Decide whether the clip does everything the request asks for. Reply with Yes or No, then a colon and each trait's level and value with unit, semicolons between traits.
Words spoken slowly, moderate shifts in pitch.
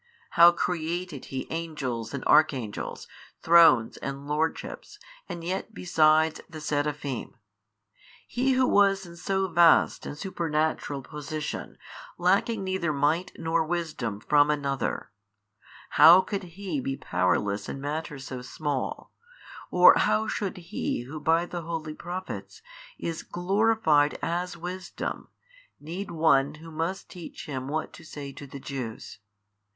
Yes: slow, 130 wpm; average, 3.6 semitones